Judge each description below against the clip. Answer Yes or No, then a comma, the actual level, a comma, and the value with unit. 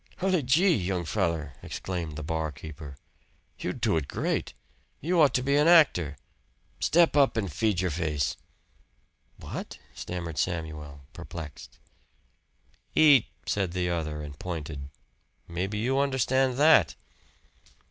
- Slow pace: Yes, slow, 125 wpm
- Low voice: Yes, very low, 90 Hz